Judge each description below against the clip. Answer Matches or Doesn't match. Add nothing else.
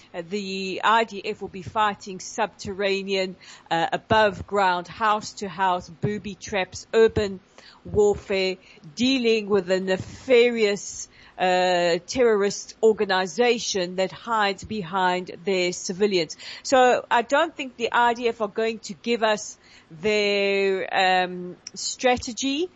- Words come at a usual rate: Doesn't match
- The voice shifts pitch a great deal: Doesn't match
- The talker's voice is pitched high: Matches